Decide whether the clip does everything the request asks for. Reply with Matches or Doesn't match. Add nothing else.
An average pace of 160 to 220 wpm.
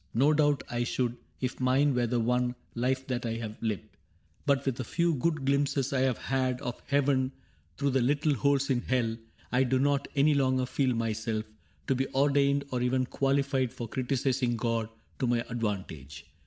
Matches